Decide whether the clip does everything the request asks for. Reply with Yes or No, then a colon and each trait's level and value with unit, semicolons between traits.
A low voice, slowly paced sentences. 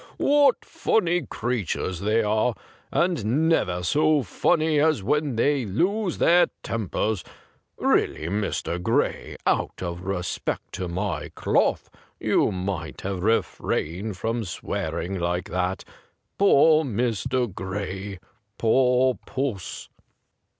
Yes: low, 110 Hz; slow, 110 wpm